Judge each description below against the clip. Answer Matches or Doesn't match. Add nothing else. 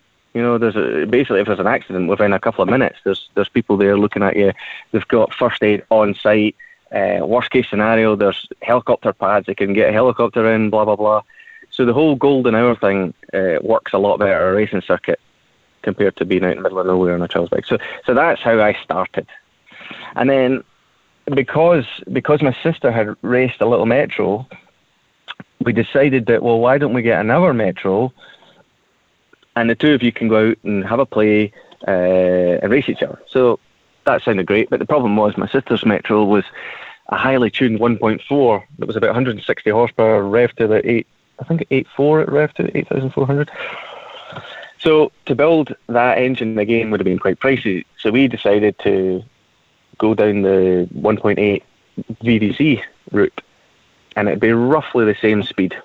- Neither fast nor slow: Matches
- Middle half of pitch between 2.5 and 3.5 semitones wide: Doesn't match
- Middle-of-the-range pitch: Doesn't match